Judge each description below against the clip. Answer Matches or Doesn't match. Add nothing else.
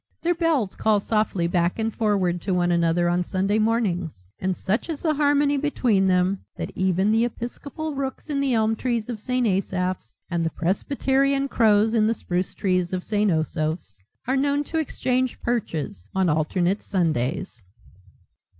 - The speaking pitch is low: Doesn't match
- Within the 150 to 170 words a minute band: Matches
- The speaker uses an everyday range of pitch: Doesn't match